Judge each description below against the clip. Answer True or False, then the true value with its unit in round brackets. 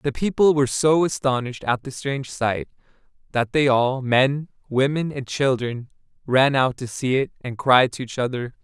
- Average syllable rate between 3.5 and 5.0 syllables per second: True (4.8 syllables/s)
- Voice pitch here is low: True (130 Hz)